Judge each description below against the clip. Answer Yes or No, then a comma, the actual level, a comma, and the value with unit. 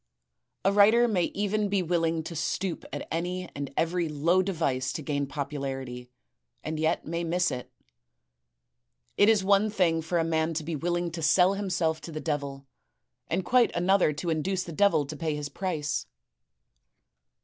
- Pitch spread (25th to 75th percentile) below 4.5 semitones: Yes, average, 3.5 semitones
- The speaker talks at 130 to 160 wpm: No, average, 170 wpm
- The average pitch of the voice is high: No, medium, 165 Hz